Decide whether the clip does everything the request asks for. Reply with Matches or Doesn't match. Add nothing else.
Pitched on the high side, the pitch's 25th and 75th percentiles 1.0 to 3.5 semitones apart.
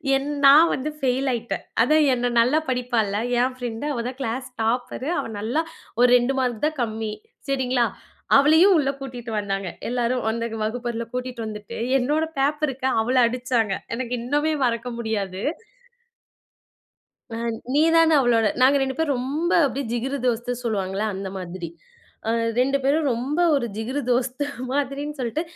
Matches